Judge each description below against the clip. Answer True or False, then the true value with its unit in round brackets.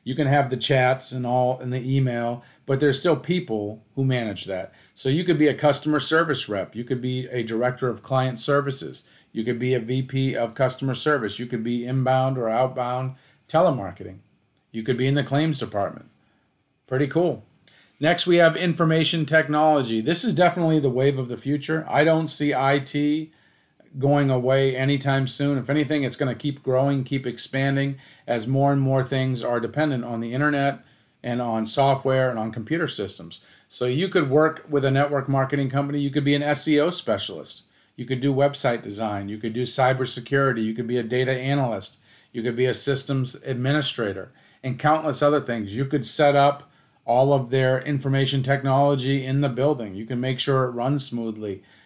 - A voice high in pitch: False (135 Hz)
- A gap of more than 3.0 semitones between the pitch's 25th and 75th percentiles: False (2.6 semitones)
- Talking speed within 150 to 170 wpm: False (190 wpm)